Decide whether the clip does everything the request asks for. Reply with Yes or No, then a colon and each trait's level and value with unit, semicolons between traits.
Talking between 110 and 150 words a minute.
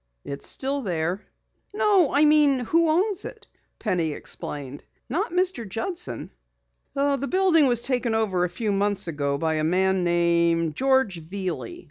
Yes: average, 145 wpm